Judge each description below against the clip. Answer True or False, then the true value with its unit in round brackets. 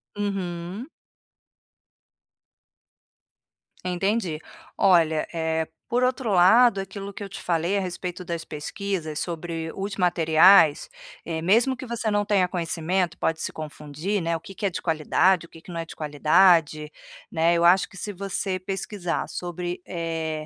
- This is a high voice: False (175 Hz)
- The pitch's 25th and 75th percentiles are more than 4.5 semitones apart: False (3.2 semitones)